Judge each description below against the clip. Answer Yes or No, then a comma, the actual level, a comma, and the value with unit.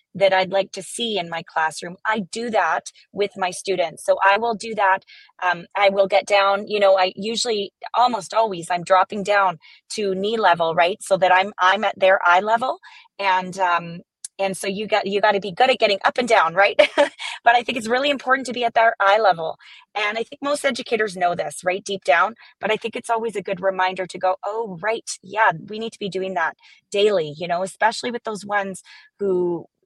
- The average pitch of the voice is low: No, high, 200 Hz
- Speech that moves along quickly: Yes, fast, 225 wpm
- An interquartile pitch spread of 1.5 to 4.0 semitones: Yes, average, 3.4 semitones